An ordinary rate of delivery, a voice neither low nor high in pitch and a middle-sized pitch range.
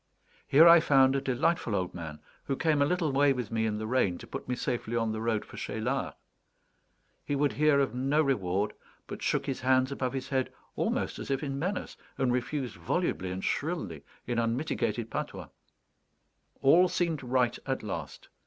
No: average, 185 wpm; low, 130 Hz; average, 4.2 semitones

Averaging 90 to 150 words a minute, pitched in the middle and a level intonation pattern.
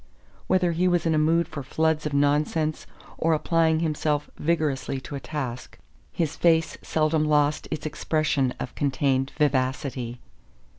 Yes: average, 145 wpm; medium, 150 Hz; narrow, 2.3 semitones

